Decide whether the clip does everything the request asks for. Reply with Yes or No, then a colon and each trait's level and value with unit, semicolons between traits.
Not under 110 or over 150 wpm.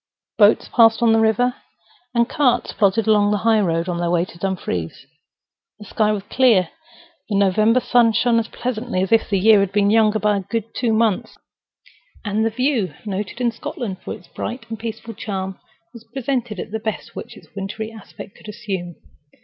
No: average, 190 wpm